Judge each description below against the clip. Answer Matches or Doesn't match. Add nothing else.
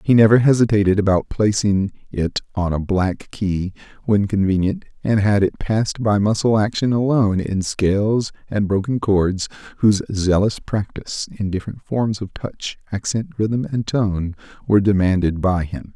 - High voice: Doesn't match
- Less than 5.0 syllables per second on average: Matches